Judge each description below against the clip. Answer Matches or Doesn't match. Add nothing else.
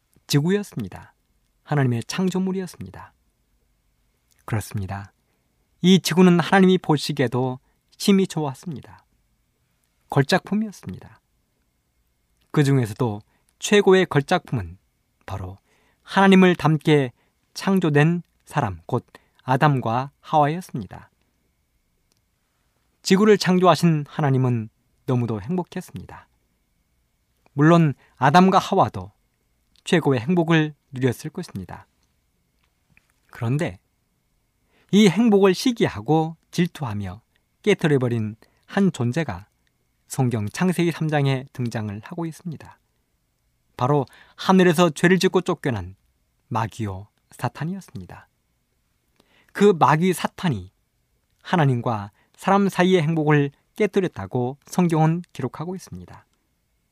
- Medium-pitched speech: Matches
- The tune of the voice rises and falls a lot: Matches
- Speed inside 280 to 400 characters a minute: Doesn't match